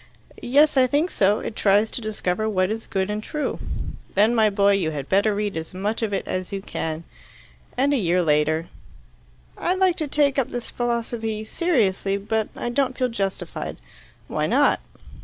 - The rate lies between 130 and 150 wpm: No, average, 180 wpm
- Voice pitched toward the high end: Yes, high, 215 Hz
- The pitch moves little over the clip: No, average, 4.1 semitones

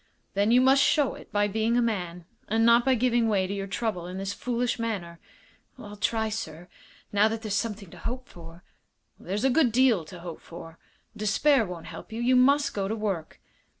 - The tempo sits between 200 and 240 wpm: Yes, fast, 205 wpm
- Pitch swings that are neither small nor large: Yes, average, 3.9 semitones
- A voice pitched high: Yes, high, 215 Hz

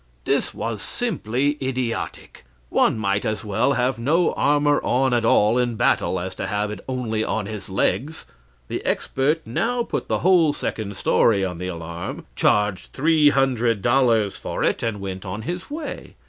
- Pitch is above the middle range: No, low, 120 Hz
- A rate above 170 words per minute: No, average, 165 wpm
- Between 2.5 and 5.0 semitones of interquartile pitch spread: No, wide, 5.5 semitones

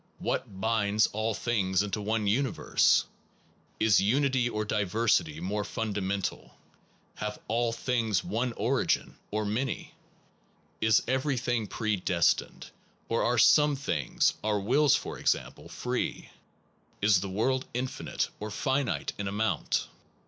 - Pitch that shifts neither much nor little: Yes, average, 3.2 semitones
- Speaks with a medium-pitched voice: No, low, 110 Hz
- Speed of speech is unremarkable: No, slow, 120 wpm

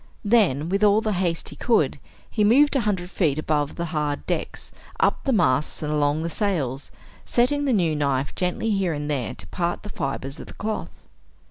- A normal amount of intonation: No, wide, 6.2 semitones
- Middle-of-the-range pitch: Yes, medium, 175 Hz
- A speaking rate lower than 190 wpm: No, average, 200 wpm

